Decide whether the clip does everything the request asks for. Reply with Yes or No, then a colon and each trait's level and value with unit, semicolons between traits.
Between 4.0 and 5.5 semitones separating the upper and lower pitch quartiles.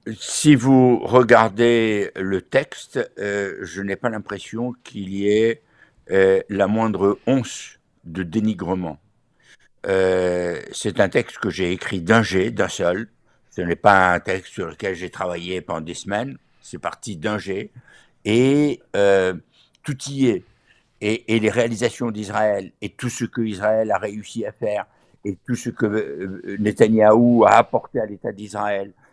No: average, 3.3 semitones